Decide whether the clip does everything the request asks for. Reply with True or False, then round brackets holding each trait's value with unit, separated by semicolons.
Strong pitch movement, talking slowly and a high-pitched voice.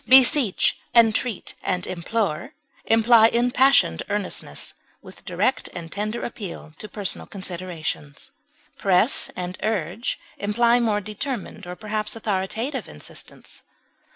False (4.2 semitones; 105 wpm; 210 Hz)